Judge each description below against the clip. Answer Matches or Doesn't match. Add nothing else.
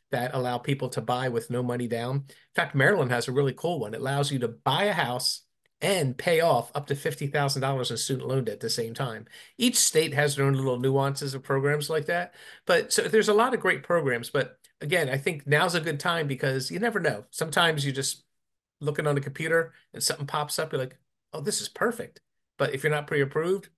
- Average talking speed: Doesn't match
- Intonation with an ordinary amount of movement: Matches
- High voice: Doesn't match